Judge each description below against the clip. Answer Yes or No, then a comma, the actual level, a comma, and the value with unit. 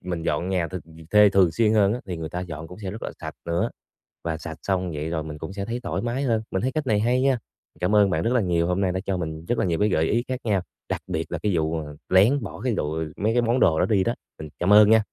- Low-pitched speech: Yes, very low, 95 Hz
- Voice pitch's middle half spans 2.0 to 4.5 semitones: No, average, 5.0 semitones